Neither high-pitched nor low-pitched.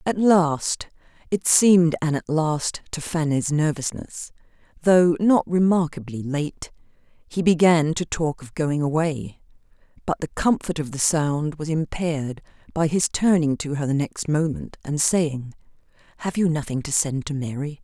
Yes: medium, 155 Hz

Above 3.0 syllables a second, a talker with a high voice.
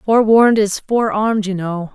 Yes: 5.5 syllables/s; high, 210 Hz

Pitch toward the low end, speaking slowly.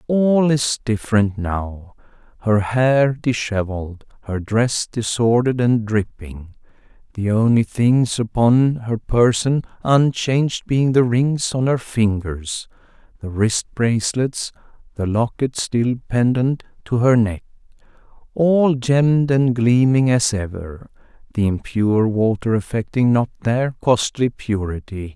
Yes: low, 115 Hz; slow, 115 wpm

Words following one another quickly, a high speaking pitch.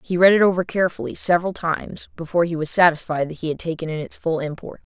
No: fast, 235 wpm; medium, 165 Hz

